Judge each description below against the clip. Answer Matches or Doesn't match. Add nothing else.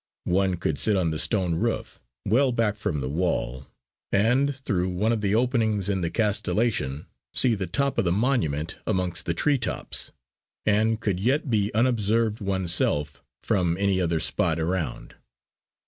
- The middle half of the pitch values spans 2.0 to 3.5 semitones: Doesn't match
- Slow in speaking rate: Doesn't match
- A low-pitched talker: Matches